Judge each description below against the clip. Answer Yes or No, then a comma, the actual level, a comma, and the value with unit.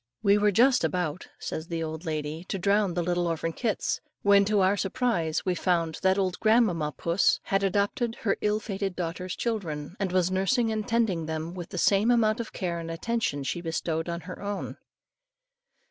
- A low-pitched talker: No, medium, 185 Hz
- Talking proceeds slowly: No, average, 185 wpm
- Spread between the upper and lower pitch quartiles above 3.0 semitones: Yes, average, 3.9 semitones